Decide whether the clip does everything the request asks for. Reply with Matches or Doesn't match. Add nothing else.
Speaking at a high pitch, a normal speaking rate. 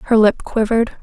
Matches